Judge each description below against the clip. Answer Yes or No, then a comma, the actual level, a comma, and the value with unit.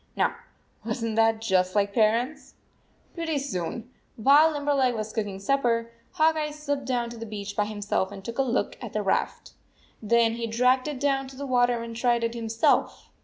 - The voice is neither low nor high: No, high, 235 Hz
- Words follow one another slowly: No, average, 195 wpm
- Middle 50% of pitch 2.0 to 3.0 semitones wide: No, average, 3.7 semitones